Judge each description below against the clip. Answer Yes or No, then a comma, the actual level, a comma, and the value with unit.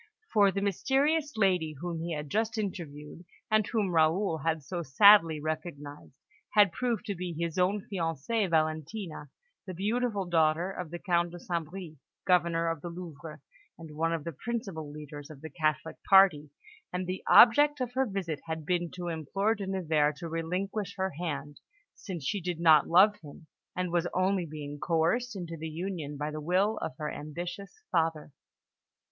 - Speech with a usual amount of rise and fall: Yes, average, 3.8 semitones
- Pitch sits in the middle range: Yes, medium, 170 Hz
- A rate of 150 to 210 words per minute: Yes, average, 175 wpm